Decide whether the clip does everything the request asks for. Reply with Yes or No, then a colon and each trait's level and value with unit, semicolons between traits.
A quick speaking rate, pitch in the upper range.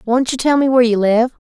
Yes: fast, 280 wpm; high, 245 Hz